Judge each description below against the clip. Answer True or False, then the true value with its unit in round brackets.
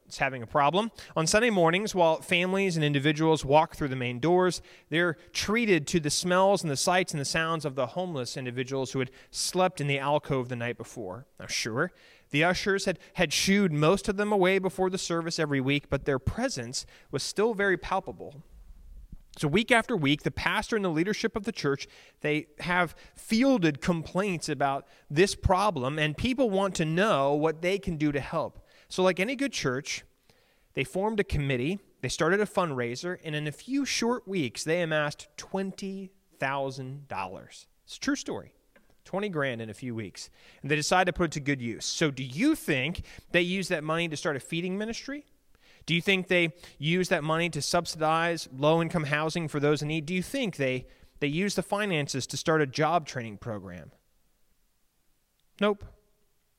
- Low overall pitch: False (165 Hz)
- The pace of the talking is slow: False (190 wpm)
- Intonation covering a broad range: False (5.0 semitones)